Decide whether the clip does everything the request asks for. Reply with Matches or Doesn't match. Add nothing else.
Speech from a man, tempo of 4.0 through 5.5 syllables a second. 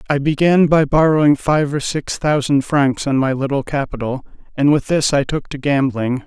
Matches